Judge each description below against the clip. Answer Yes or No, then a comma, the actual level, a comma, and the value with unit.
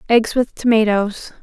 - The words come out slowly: Yes, slow, 125 wpm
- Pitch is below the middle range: No, high, 220 Hz